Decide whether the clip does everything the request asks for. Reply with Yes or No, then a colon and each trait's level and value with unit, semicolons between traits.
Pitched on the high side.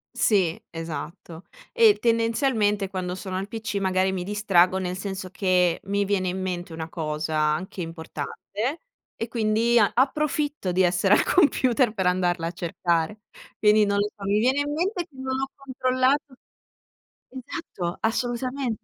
Yes: high, 200 Hz